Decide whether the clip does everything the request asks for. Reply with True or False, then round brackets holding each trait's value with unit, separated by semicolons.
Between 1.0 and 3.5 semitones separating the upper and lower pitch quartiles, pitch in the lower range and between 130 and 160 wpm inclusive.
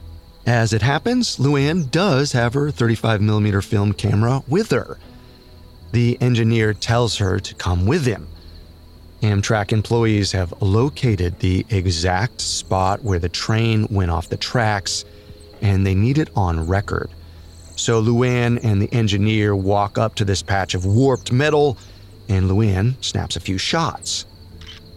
False (4.0 semitones; 105 Hz; 140 wpm)